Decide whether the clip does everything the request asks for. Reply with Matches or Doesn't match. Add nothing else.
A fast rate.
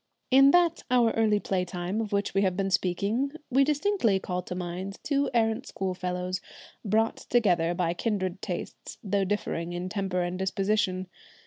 Doesn't match